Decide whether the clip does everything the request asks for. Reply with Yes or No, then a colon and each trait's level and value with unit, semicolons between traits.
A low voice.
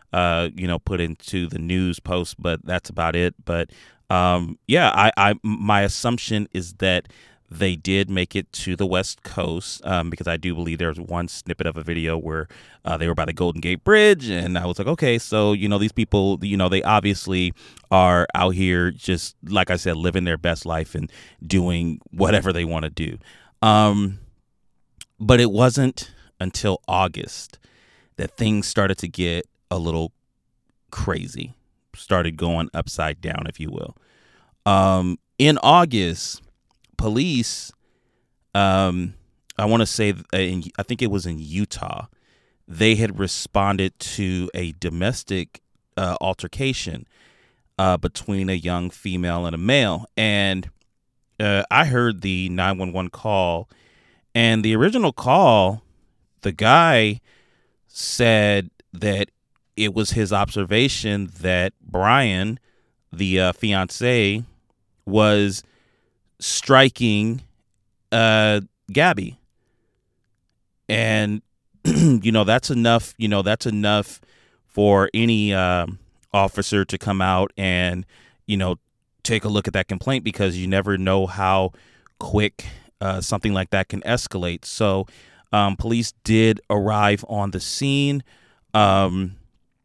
Yes: low, 100 Hz